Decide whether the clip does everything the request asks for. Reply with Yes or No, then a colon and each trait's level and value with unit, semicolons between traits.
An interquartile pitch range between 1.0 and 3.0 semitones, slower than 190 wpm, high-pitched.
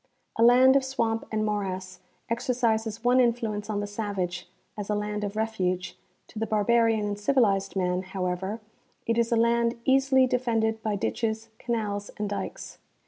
Yes: narrow, 2.5 semitones; average, 160 wpm; high, 220 Hz